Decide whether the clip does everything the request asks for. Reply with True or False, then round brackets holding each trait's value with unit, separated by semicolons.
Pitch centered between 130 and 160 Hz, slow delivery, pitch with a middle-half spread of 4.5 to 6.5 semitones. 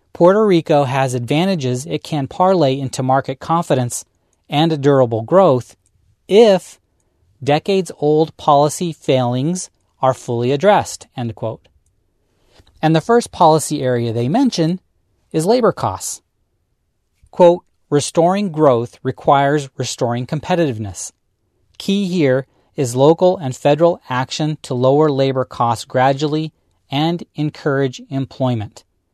True (140 Hz; 110 wpm; 4.8 semitones)